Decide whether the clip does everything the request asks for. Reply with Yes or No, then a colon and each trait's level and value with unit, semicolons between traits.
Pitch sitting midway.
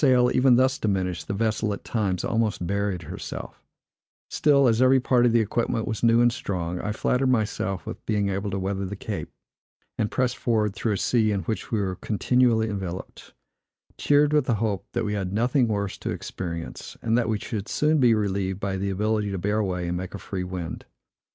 No: low, 105 Hz